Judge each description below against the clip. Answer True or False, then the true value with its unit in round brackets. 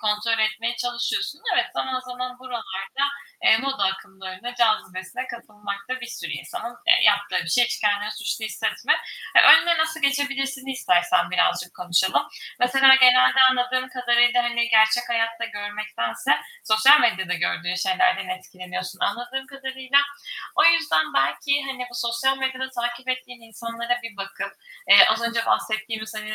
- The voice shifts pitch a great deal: False (3.5 semitones)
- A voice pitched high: True (235 Hz)